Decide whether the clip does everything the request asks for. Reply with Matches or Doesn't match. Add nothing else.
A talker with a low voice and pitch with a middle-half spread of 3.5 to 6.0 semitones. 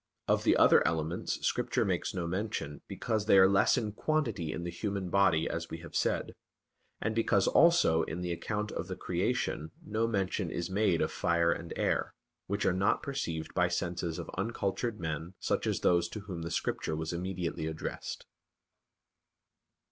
Matches